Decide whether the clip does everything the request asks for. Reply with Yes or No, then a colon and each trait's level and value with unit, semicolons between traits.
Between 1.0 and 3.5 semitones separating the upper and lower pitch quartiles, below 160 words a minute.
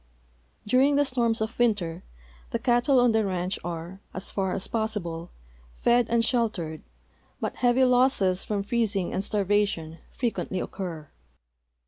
No: average, 4.8 semitones; average, 140 wpm